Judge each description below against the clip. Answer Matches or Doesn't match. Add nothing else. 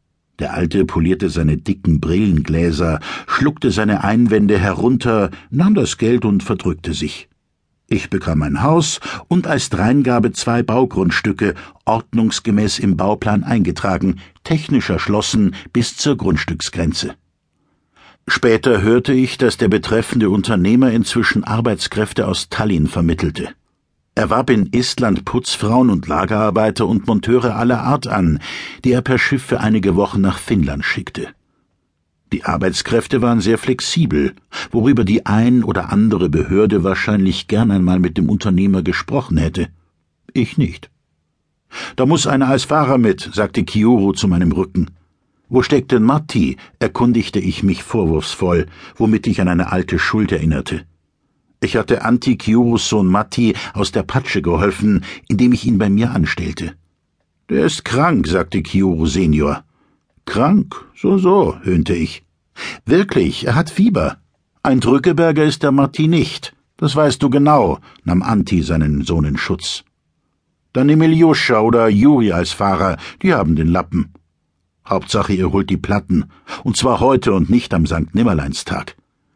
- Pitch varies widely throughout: Matches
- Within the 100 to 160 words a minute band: Matches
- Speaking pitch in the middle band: Doesn't match